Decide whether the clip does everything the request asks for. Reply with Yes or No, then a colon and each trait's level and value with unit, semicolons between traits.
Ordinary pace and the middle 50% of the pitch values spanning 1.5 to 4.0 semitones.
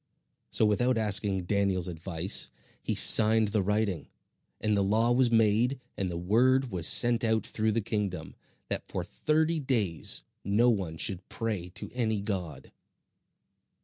Yes: average, 145 wpm; average, 3.5 semitones